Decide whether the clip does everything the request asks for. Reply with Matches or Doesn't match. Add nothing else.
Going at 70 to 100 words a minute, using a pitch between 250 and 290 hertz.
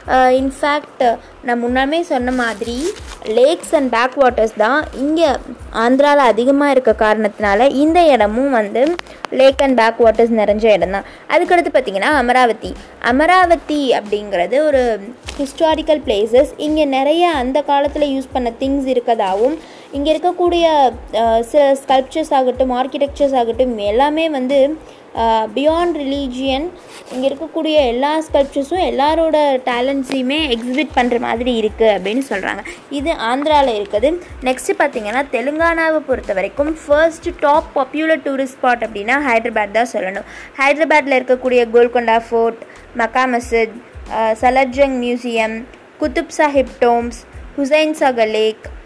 Doesn't match